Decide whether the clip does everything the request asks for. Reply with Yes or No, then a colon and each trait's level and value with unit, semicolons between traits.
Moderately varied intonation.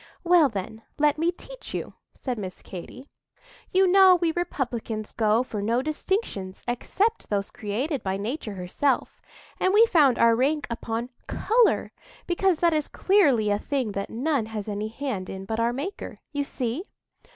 No: wide, 7.6 semitones